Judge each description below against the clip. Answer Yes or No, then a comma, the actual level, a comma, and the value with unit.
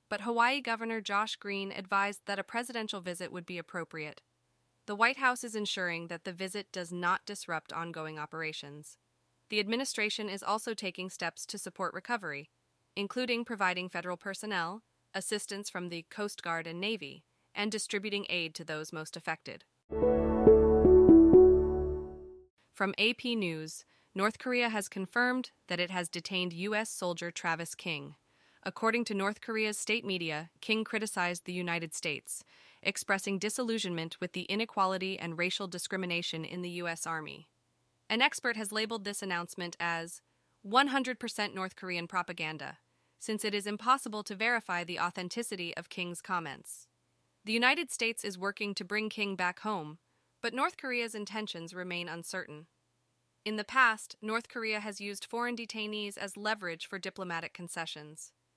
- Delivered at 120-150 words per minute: Yes, average, 145 wpm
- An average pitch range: Yes, average, 4.1 semitones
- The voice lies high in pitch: Yes, high, 195 Hz